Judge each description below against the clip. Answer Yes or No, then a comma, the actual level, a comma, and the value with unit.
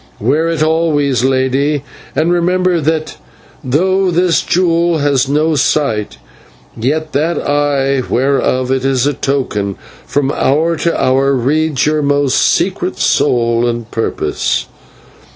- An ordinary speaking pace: No, slow, 125 wpm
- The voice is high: No, medium, 145 Hz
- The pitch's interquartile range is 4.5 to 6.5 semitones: No, average, 3.4 semitones